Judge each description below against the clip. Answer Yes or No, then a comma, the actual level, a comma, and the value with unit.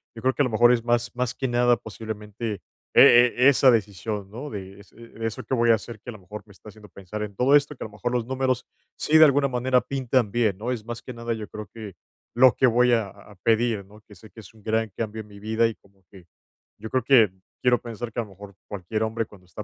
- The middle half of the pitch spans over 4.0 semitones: No, average, 2.8 semitones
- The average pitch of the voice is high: No, low, 115 Hz